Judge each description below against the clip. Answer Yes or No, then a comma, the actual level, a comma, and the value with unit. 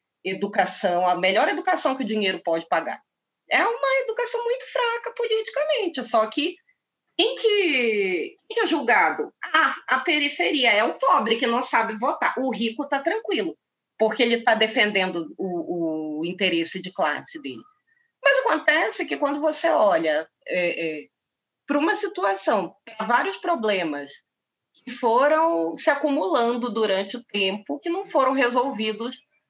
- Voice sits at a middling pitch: No, very high, 260 Hz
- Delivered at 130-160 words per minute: Yes, average, 145 wpm